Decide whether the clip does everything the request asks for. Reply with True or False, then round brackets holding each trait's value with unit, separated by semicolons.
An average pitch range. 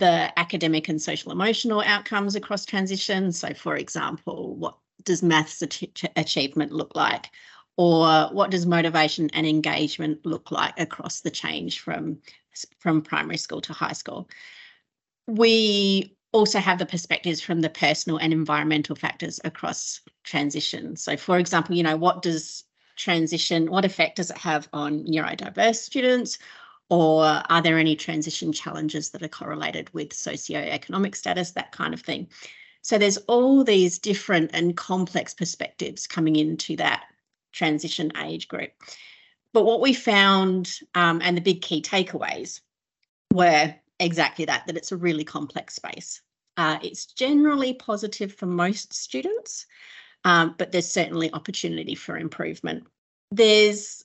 True (4.2 semitones)